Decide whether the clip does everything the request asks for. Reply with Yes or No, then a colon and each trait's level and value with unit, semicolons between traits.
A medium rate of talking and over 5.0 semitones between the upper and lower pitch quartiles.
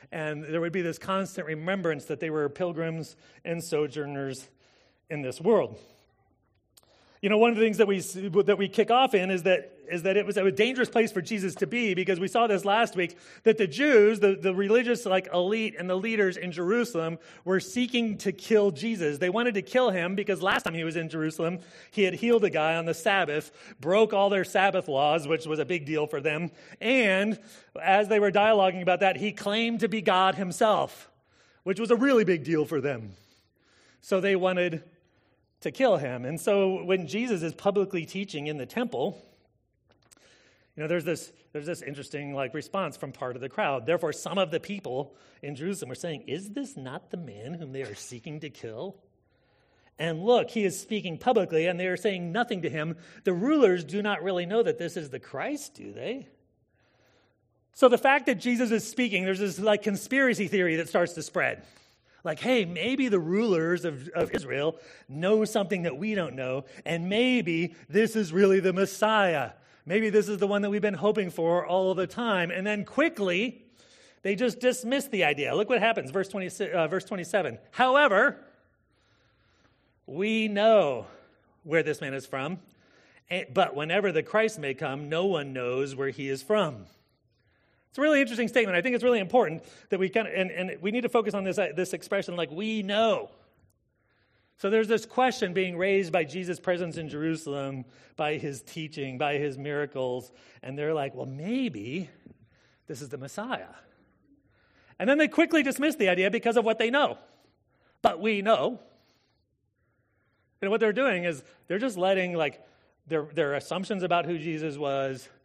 Yes: average, 190 wpm; wide, 5.6 semitones